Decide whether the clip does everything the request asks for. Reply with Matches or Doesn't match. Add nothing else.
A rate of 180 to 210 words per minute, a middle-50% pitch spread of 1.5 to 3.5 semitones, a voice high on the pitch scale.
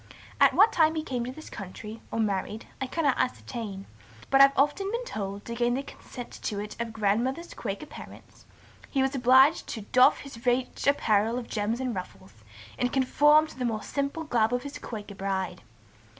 Doesn't match